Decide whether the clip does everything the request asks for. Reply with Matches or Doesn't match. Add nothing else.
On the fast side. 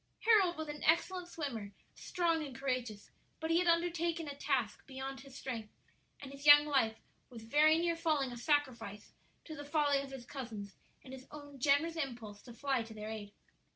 Doesn't match